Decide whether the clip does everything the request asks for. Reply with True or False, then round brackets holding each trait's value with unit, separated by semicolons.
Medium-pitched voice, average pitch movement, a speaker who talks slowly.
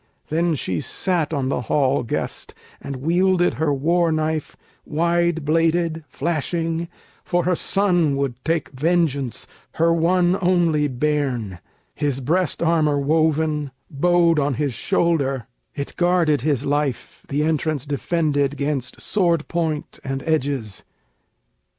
True (155 Hz; 3.3 semitones; 125 wpm)